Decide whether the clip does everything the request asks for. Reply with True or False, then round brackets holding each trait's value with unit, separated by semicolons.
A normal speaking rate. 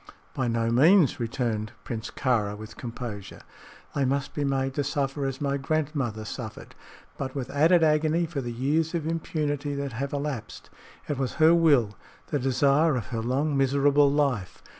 True (165 wpm)